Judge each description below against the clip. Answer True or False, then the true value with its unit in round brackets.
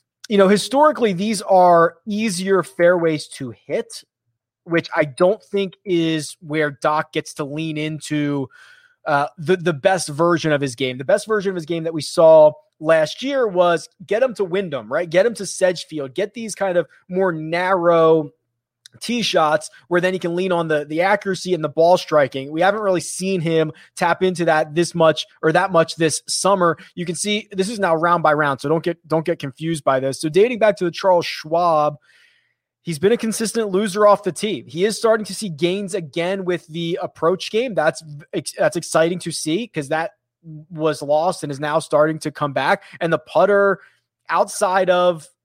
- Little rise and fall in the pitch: False (3.7 semitones)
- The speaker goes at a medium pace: True (195 wpm)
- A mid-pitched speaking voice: True (170 Hz)